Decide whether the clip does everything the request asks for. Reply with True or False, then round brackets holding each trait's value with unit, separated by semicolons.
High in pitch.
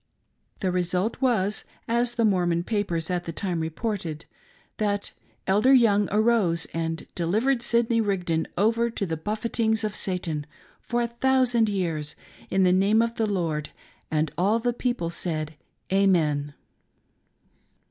True (195 Hz)